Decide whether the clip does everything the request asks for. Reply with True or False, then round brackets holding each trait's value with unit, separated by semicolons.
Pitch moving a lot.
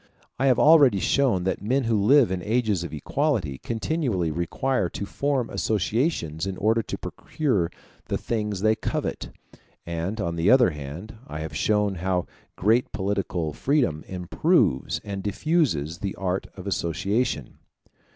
True (5.9 semitones)